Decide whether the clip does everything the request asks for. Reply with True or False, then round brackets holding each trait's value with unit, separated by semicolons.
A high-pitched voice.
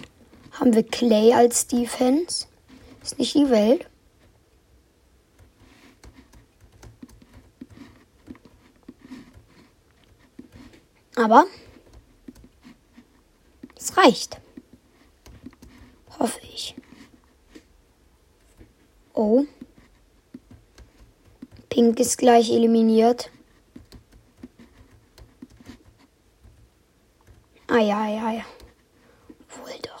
True (240 Hz)